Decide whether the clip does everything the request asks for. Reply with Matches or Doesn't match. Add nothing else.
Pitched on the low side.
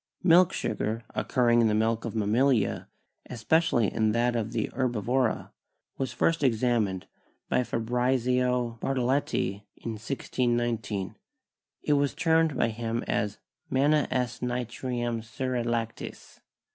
Matches